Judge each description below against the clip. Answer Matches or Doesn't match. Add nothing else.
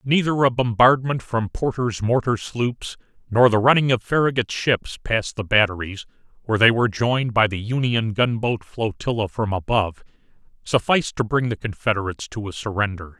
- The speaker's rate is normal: Matches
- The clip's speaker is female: Doesn't match